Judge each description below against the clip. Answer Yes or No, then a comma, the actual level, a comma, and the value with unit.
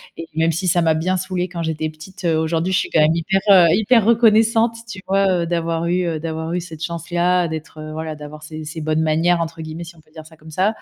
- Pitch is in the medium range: Yes, medium, 165 Hz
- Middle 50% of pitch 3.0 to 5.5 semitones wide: No, narrow, 2.5 semitones